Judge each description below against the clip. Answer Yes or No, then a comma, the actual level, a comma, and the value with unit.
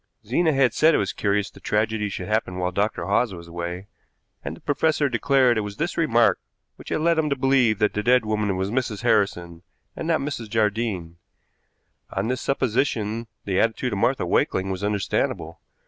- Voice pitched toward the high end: No, low, 110 Hz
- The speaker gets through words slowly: No, average, 190 wpm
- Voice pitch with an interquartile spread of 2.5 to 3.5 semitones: No, average, 4.6 semitones